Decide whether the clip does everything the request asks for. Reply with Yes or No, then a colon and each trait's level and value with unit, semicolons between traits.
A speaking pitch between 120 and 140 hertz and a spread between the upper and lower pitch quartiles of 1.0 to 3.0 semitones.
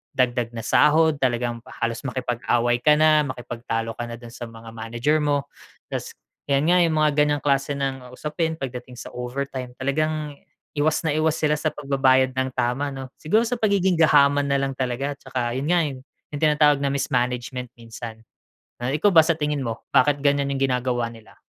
No: low, 135 Hz; average, 3.4 semitones